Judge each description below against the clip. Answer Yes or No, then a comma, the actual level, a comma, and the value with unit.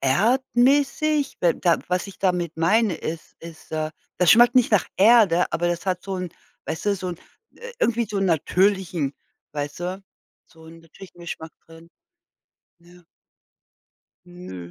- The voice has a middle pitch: Yes, medium, 180 Hz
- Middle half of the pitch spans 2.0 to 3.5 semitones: No, average, 4.0 semitones